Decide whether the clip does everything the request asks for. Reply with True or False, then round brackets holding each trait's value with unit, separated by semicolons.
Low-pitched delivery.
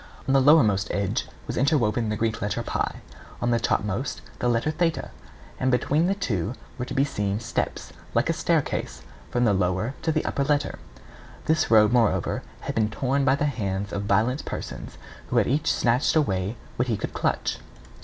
True (120 Hz)